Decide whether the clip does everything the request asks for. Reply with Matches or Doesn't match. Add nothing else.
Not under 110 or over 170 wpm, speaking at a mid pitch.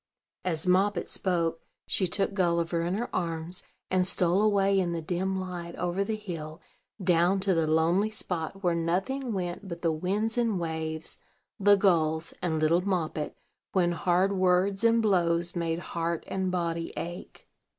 Matches